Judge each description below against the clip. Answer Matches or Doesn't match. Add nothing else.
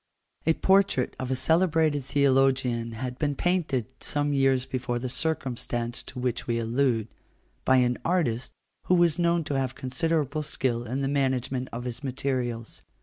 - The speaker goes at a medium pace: Matches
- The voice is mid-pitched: Doesn't match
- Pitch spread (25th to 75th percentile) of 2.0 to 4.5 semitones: Matches